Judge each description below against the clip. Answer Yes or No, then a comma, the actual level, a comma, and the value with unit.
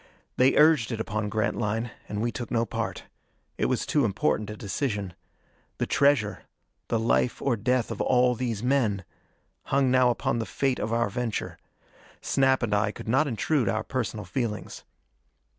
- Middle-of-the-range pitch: No, low, 115 Hz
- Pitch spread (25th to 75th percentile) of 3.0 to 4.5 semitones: Yes, average, 3.3 semitones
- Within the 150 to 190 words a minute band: Yes, average, 165 wpm